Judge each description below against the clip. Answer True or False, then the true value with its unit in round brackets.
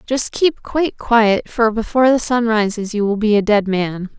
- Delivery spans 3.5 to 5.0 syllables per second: True (4.8 syllables/s)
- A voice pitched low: False (225 Hz)